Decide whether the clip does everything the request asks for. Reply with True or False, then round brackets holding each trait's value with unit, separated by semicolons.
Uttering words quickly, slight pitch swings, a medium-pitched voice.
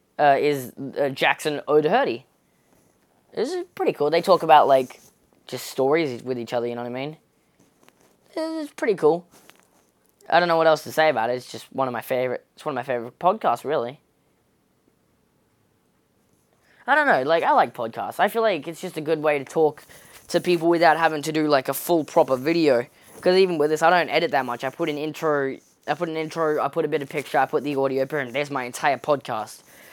False (220 wpm; 3.8 semitones; 155 Hz)